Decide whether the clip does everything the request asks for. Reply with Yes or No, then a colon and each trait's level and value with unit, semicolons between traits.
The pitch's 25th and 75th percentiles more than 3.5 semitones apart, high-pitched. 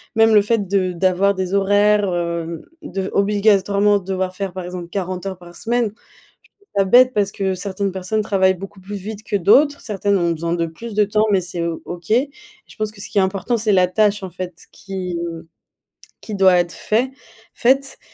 No: narrow, 2.6 semitones; high, 195 Hz